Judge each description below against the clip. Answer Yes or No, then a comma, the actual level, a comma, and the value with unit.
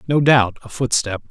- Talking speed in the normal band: Yes, average, 185 wpm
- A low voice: Yes, low, 125 Hz